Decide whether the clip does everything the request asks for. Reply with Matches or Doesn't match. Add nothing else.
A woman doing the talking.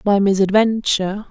Matches